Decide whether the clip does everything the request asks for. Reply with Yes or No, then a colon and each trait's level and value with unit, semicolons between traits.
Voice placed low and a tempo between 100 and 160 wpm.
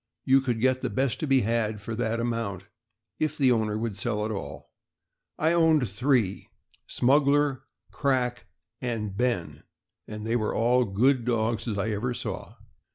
No: low, 120 Hz; average, 170 wpm